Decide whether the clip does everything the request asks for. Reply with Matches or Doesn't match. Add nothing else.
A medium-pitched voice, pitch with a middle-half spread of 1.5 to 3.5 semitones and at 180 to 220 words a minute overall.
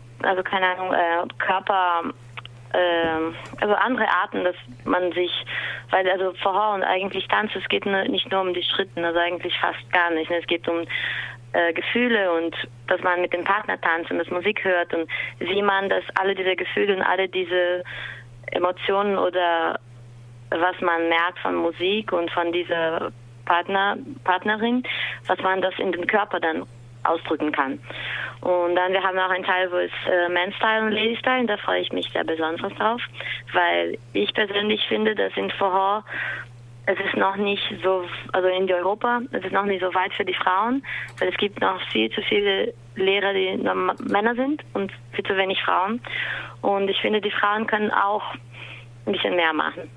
Matches